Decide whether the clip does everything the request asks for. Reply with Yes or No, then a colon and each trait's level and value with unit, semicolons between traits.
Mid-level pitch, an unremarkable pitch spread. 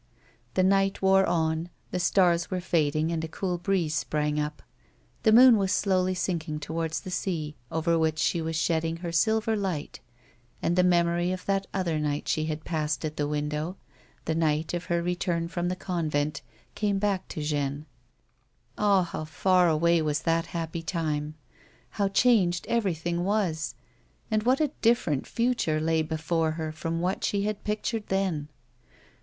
Yes: medium, 170 Hz; average, 3.3 semitones